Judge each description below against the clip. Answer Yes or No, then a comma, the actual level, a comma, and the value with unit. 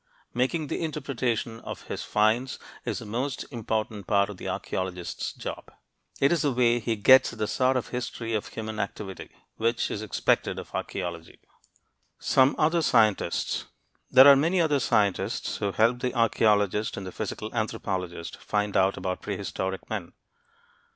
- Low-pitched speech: Yes, low, 110 Hz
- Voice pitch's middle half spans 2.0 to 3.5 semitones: No, average, 4.1 semitones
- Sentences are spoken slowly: No, average, 155 wpm